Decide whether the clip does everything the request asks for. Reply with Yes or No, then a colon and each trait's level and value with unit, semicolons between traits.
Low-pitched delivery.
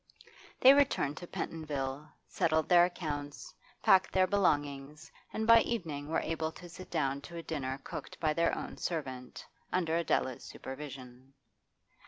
No: medium, 155 Hz